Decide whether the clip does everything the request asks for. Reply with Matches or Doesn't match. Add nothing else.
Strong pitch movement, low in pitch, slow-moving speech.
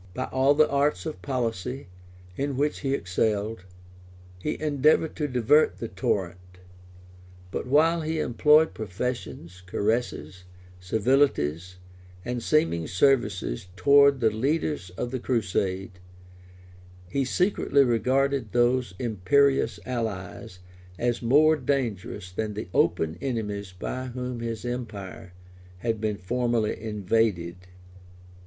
Matches